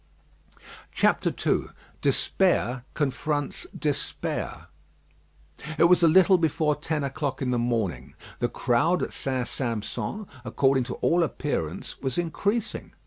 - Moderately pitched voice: Yes, medium, 145 Hz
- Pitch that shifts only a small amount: No, average, 5.2 semitones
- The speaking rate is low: Yes, slow, 115 wpm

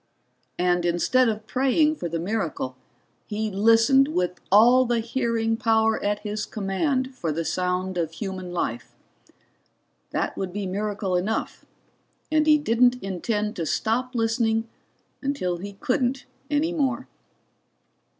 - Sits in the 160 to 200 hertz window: No, high, 220 Hz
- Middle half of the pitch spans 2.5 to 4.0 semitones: No, average, 5.2 semitones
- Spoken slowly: Yes, slow, 130 wpm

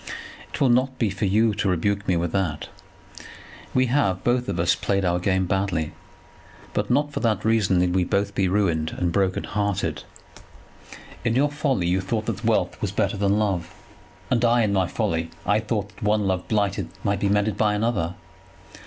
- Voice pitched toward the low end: Yes, low, 100 Hz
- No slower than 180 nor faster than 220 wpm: Yes, average, 190 wpm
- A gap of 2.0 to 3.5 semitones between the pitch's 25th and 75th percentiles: Yes, average, 3.2 semitones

